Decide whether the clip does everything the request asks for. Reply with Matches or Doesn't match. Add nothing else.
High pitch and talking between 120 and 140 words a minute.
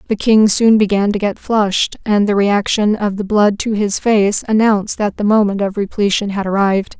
Doesn't match